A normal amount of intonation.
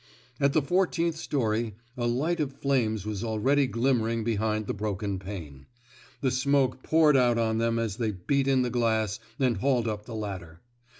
Yes: average, 4.0 semitones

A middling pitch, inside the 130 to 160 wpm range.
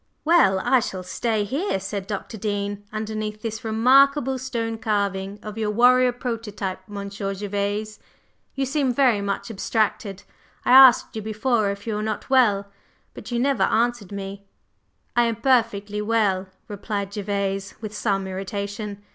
No: high, 210 Hz; average, 145 wpm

